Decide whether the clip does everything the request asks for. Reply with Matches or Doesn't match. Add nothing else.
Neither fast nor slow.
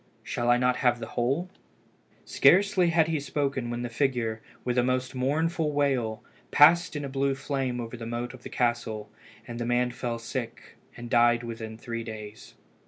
Matches